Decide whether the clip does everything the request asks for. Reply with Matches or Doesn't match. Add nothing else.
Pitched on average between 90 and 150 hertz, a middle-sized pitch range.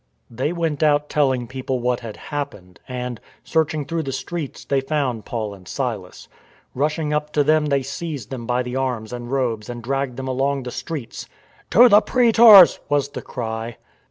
Matches